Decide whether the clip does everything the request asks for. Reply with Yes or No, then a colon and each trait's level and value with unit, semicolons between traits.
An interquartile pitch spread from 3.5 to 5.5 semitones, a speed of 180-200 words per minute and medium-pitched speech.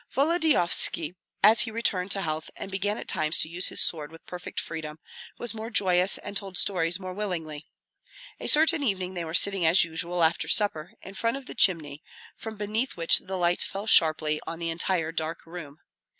Yes: average, 3.9 semitones; average, 195 wpm; medium, 180 Hz